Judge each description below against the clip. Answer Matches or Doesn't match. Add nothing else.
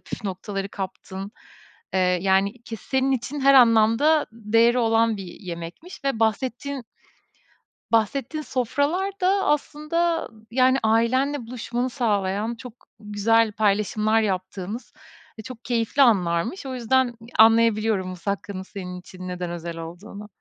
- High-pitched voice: Matches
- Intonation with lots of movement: Doesn't match